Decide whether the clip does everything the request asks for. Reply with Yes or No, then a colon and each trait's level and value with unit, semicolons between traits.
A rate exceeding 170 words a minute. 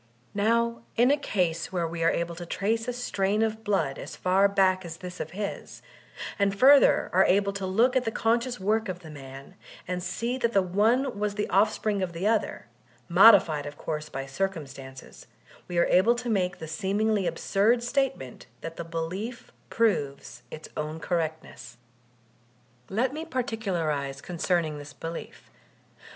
No: average, 165 wpm